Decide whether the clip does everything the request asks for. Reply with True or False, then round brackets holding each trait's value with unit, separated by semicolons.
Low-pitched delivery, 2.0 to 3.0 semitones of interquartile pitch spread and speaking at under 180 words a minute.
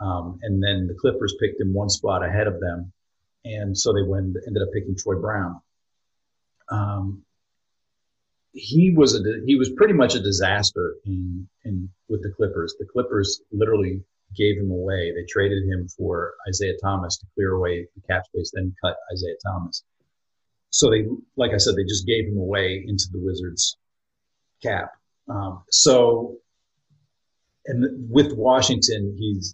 True (100 Hz; 2.5 semitones; 160 wpm)